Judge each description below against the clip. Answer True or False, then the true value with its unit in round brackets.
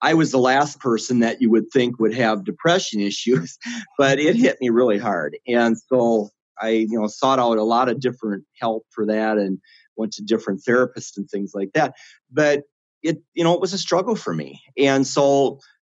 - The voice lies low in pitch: True (120 Hz)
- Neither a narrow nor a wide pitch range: True (4.2 semitones)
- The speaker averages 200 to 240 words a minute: True (205 wpm)